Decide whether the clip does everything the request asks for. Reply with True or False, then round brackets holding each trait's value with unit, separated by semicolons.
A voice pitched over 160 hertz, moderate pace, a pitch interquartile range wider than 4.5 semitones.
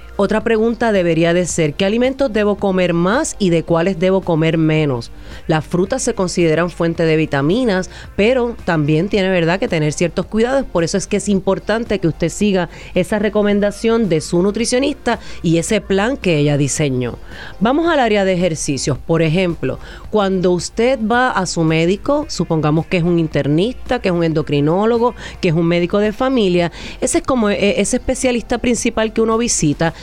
True (190 Hz; 175 wpm; 5.3 semitones)